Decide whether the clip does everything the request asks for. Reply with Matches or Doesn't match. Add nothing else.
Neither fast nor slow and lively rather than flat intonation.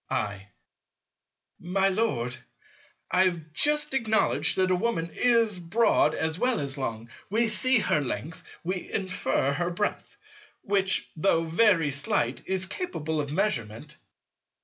Doesn't match